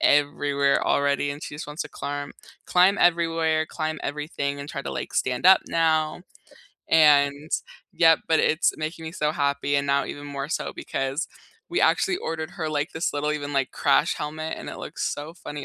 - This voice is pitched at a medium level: Yes, medium, 150 Hz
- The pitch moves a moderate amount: No, narrow, 2.1 semitones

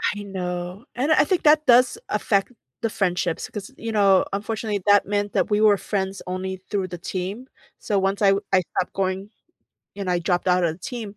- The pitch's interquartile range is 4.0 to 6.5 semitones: No, narrow, 2.5 semitones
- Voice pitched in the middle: No, high, 200 Hz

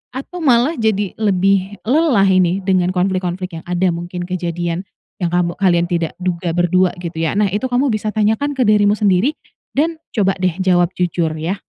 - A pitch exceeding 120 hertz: Yes, medium, 185 Hz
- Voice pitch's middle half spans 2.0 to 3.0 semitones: No, average, 3.4 semitones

